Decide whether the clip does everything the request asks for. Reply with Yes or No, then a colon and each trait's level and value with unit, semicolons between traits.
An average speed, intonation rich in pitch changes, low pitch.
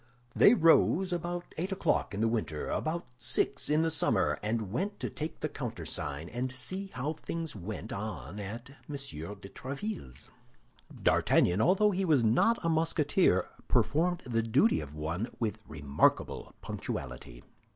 Yes: average, 145 wpm; wide, 9.0 semitones; low, 125 Hz